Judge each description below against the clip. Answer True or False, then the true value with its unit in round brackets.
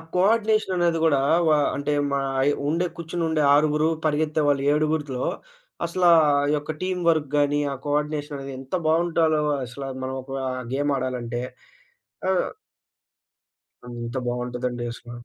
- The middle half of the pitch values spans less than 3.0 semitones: False (3.3 semitones)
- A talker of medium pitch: True (145 Hz)